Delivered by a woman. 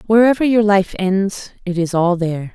Yes: female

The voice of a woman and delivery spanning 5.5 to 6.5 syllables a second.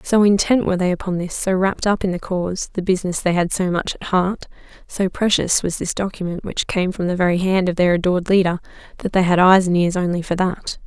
Yes: female; 5.9 syllables/s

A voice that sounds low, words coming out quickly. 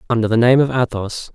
Yes: low, 120 Hz; fast, 225 wpm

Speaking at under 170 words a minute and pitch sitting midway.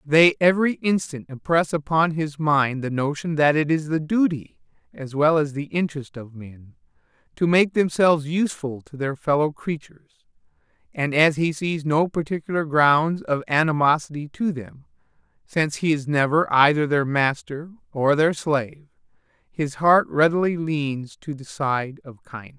Yes: average, 155 wpm; medium, 150 Hz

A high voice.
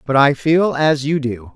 No: medium, 145 Hz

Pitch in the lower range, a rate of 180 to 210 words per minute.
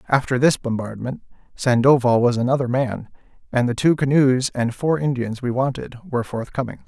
No: low, 125 Hz; average, 155 wpm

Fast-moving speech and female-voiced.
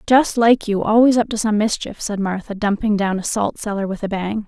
Yes: fast, 240 wpm; female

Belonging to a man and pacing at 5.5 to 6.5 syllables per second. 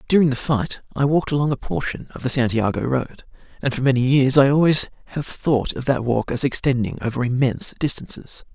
Yes: male; 5.7 syllables/s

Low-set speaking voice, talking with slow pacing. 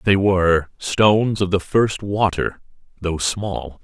Yes: very low, 95 Hz; slow, 125 wpm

